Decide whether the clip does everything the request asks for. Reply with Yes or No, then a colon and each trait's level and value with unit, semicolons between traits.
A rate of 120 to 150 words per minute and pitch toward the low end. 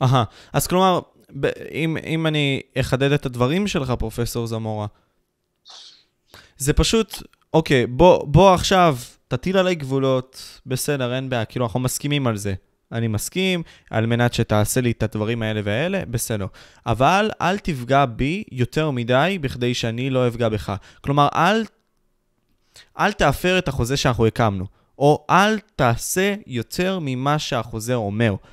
Yes: average, 140 wpm; low, 130 Hz